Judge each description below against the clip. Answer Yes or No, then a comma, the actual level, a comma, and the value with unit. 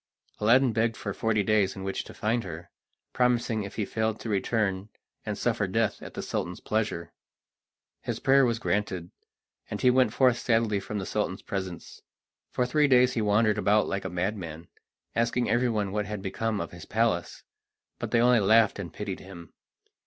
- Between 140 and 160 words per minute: No, average, 180 wpm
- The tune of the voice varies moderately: Yes, average, 3.3 semitones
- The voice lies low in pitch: Yes, low, 105 Hz